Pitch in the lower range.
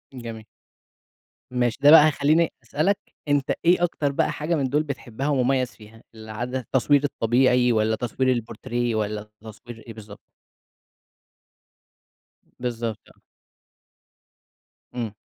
Yes: low, 125 Hz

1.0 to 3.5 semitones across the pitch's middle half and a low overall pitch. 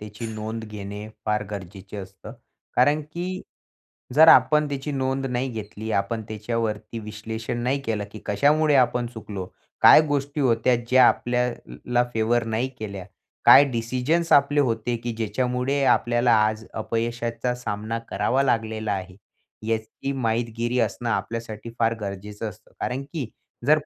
Yes: average, 3.1 semitones; low, 115 Hz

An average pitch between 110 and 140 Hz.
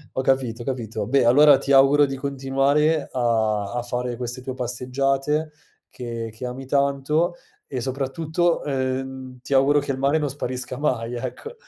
Yes: low, 135 Hz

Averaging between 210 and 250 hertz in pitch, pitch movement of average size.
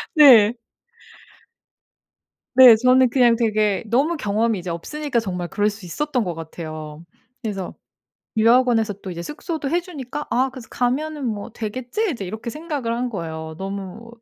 Yes: high, 230 Hz; average, 4.9 semitones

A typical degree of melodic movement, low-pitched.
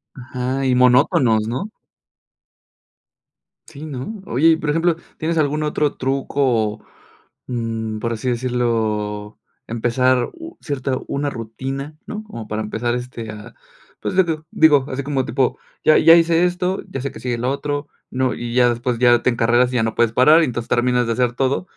Yes: average, 3.6 semitones; low, 125 Hz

